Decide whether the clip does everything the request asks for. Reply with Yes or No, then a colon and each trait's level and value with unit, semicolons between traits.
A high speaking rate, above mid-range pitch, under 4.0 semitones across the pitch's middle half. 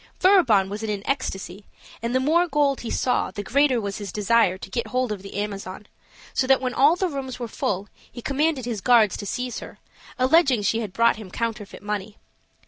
No: fast, 210 wpm; high, 230 Hz; average, 4.4 semitones